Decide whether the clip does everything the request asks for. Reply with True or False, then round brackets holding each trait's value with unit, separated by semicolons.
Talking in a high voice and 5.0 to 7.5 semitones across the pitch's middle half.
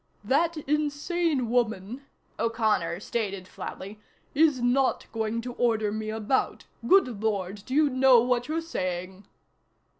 False (235 Hz; 4.6 semitones)